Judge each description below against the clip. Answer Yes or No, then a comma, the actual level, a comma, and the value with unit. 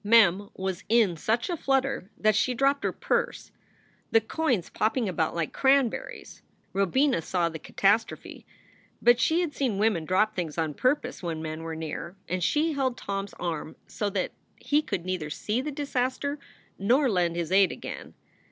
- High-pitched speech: Yes, high, 210 Hz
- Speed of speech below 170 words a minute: No, average, 175 wpm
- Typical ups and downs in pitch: No, wide, 6.9 semitones